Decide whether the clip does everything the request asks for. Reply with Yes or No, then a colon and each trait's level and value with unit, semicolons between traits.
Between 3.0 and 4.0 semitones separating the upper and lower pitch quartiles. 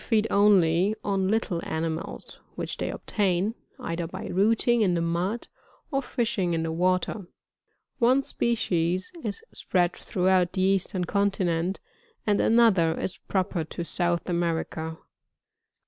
Yes: average, 3.3 semitones